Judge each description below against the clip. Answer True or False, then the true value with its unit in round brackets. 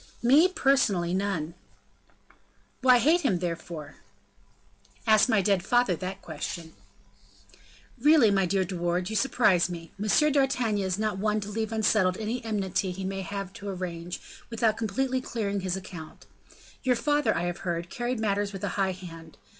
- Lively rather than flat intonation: False (4.1 semitones)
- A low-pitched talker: False (200 Hz)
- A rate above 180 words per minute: False (160 wpm)